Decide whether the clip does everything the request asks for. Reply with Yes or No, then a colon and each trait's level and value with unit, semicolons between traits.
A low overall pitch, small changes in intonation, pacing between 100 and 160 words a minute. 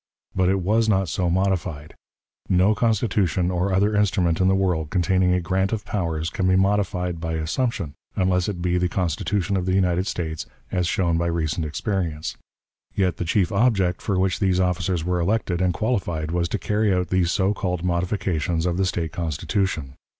No: very low, 90 Hz; narrow, 2.2 semitones; average, 185 wpm